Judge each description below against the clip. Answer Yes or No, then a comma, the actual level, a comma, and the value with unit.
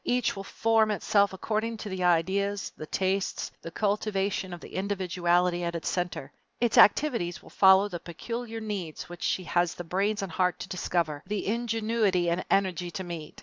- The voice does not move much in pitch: No, average, 3.1 semitones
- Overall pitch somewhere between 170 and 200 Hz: Yes, high, 190 Hz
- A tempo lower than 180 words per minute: No, average, 185 wpm